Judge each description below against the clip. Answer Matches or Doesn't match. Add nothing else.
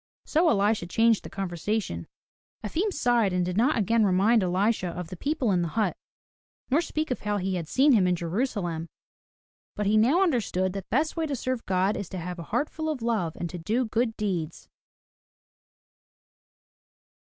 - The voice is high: Matches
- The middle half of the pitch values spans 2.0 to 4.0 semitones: Doesn't match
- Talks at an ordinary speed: Matches